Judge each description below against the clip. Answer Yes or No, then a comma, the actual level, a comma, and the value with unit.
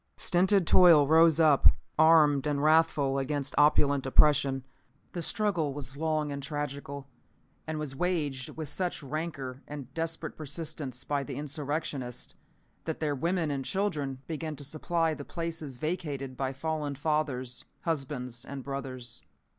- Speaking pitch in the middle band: Yes, medium, 145 Hz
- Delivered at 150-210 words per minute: No, average, 140 wpm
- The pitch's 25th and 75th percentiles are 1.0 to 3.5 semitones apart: Yes, average, 2.8 semitones